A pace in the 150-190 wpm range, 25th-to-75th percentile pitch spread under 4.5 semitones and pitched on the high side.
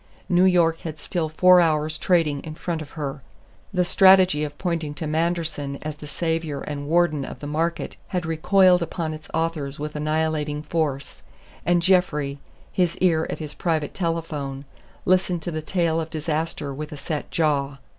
No: average, 170 wpm; narrow, 2.4 semitones; medium, 160 Hz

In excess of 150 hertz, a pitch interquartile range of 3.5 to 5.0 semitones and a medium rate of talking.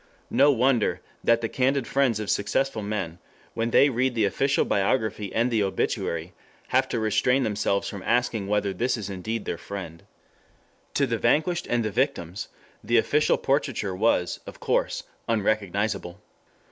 No: low, 110 Hz; average, 3.9 semitones; average, 160 wpm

